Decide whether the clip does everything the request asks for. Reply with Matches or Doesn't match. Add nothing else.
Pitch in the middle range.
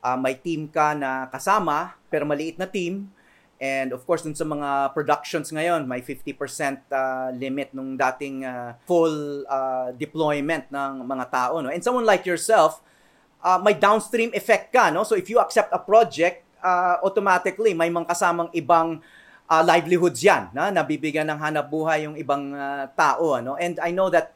Matches